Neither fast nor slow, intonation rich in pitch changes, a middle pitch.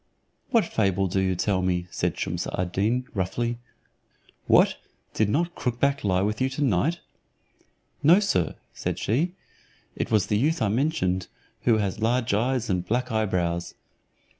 No: average, 155 wpm; wide, 5.8 semitones; low, 110 Hz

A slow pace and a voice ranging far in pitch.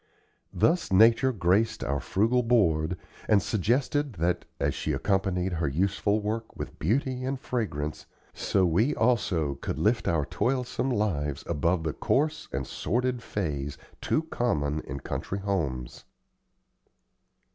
Yes: slow, 130 wpm; wide, 7.2 semitones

